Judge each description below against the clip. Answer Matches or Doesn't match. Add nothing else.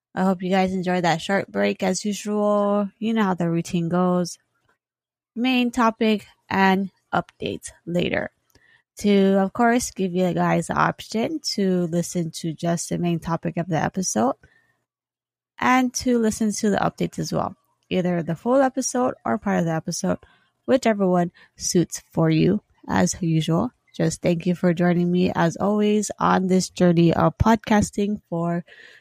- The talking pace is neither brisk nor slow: Matches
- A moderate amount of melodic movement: Matches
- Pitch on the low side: Doesn't match